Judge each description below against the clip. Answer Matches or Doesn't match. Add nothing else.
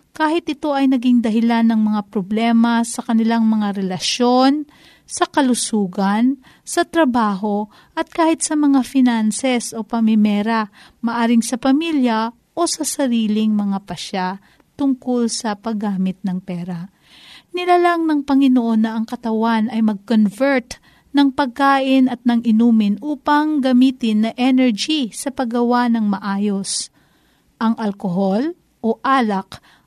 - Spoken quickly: Doesn't match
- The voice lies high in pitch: Matches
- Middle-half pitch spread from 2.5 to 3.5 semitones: Doesn't match